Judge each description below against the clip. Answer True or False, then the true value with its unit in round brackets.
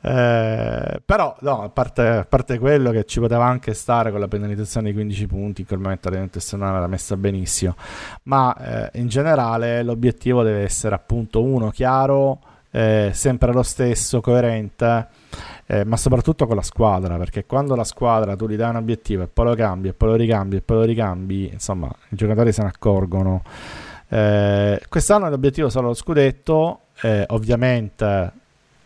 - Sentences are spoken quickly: True (175 wpm)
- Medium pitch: False (110 Hz)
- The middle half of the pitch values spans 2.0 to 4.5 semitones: True (3.6 semitones)